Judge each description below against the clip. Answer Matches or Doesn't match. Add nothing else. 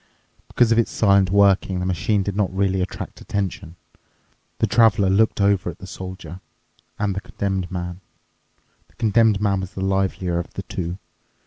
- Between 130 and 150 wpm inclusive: Doesn't match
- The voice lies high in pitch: Doesn't match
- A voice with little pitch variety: Matches